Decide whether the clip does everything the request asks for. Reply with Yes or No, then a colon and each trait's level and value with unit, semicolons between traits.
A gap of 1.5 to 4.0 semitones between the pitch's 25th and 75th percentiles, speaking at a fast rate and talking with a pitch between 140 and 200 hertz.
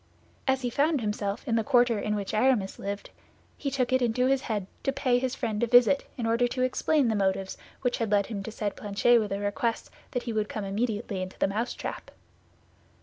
No: average, 3.5 semitones; fast, 215 wpm; high, 230 Hz